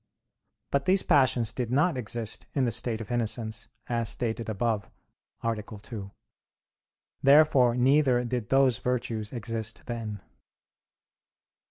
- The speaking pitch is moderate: No, low, 120 Hz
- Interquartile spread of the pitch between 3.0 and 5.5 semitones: No, narrow, 2.5 semitones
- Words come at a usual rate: No, slow, 120 wpm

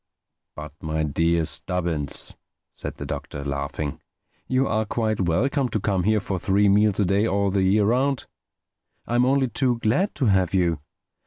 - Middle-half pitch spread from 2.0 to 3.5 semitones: No, average, 5.3 semitones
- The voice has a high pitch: No, low, 100 Hz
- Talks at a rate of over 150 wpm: Yes, average, 165 wpm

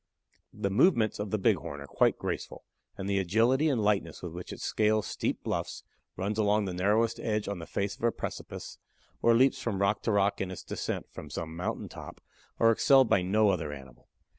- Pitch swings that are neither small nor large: Yes, average, 3.3 semitones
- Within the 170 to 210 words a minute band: Yes, fast, 205 wpm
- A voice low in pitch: Yes, low, 100 Hz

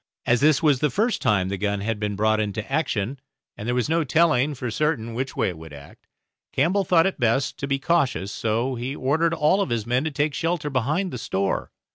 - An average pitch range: No, wide, 6.1 semitones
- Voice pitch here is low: Yes, low, 130 Hz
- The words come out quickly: Yes, fast, 220 wpm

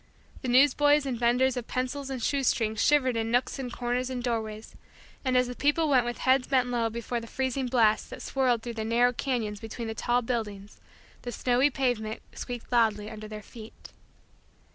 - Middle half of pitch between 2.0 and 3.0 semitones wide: Yes, narrow, 2.4 semitones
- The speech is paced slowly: No, average, 185 wpm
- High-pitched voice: Yes, high, 245 Hz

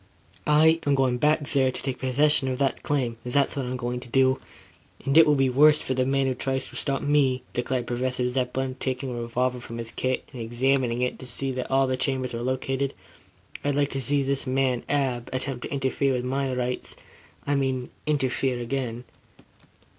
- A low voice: Yes, low, 130 Hz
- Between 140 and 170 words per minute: No, fast, 205 wpm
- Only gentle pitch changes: Yes, narrow, 1.6 semitones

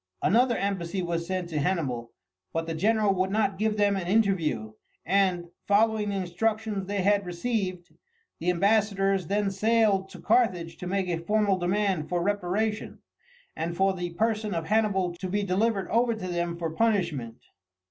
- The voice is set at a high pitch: Yes, high, 195 Hz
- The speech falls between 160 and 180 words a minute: Yes, average, 165 wpm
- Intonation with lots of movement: No, average, 3.2 semitones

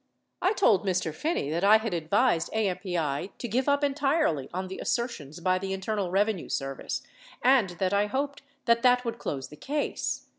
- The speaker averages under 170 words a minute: No, average, 180 wpm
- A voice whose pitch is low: No, high, 200 Hz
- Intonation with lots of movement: Yes, wide, 6.1 semitones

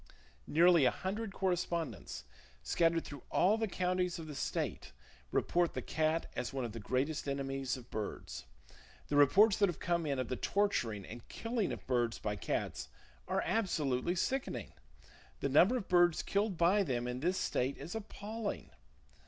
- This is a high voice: No, medium, 165 Hz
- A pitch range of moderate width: No, wide, 6.6 semitones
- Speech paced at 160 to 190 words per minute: Yes, average, 165 wpm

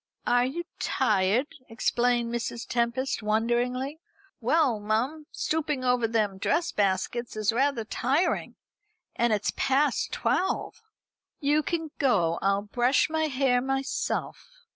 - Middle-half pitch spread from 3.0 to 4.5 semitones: Yes, average, 3.9 semitones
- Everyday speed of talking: No, slow, 120 wpm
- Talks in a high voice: Yes, high, 245 Hz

